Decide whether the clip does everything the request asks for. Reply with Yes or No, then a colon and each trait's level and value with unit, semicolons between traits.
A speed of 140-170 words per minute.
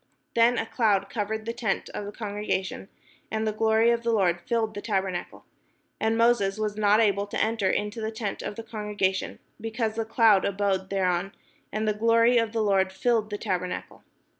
No: average, 190 wpm